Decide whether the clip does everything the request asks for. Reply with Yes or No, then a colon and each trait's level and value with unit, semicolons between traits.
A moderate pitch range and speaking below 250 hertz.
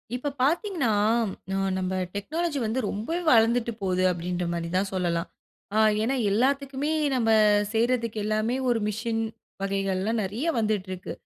Yes: average, 4.8 semitones; high, 220 Hz